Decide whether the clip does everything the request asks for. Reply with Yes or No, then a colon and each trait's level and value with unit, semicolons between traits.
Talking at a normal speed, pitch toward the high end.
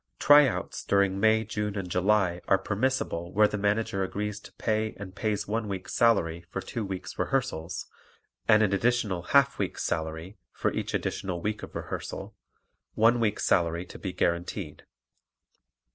No: average, 155 wpm; low, 100 Hz